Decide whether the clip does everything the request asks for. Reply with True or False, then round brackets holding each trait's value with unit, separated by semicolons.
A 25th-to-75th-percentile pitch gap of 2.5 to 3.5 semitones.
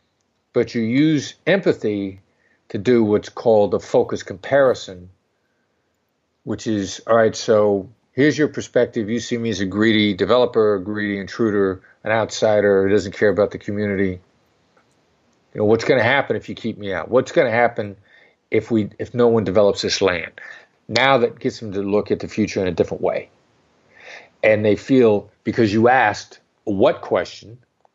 True (2.8 semitones)